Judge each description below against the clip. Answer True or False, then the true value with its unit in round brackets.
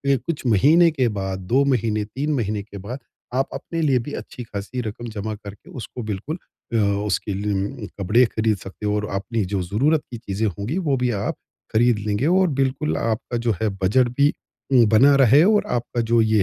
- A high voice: False (115 Hz)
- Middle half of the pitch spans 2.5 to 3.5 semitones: False (4.6 semitones)